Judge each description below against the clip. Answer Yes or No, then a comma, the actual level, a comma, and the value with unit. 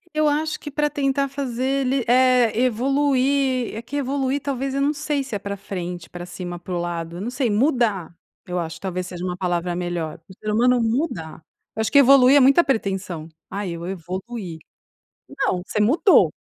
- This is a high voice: Yes, high, 230 Hz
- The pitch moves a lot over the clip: Yes, wide, 7.2 semitones